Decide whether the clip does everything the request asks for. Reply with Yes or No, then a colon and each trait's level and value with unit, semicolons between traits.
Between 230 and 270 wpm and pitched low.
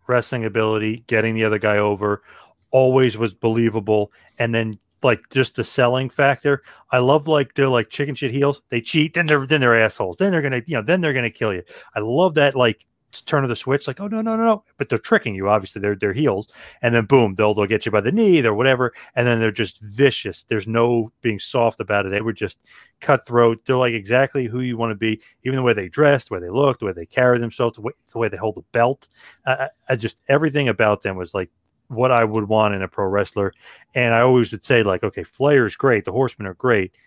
Yes: fast, 245 wpm; low, 120 Hz